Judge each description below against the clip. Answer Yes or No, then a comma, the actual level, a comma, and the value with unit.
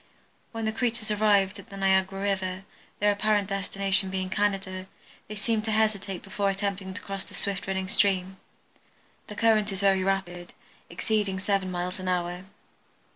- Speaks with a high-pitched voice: Yes, high, 195 Hz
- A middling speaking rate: Yes, average, 160 wpm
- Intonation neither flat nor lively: No, narrow, 1.6 semitones